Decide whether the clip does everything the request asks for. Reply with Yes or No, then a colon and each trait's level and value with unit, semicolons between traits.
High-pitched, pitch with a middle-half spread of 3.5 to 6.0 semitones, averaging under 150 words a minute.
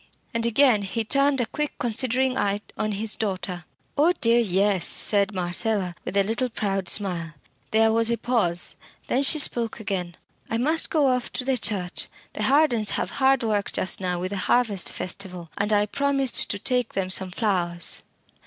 No: high, 215 Hz; average, 4.6 semitones; average, 180 wpm